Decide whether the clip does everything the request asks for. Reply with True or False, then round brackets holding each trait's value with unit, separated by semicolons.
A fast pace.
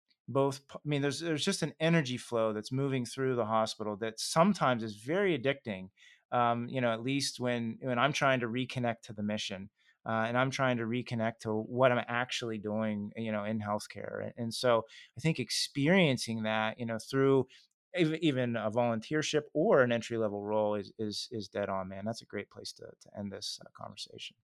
False (195 wpm)